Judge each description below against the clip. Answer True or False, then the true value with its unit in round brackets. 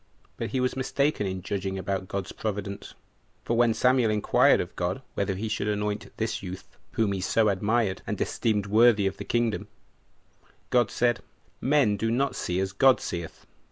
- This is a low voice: True (105 Hz)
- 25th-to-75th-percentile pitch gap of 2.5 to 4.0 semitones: True (3.6 semitones)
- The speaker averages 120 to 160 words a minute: False (175 wpm)